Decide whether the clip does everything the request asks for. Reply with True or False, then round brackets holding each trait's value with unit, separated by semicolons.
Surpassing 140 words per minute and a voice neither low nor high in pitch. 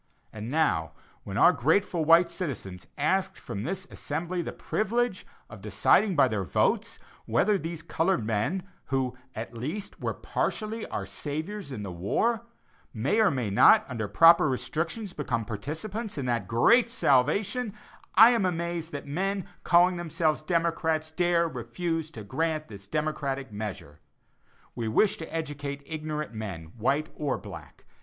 True (150 wpm; 155 Hz)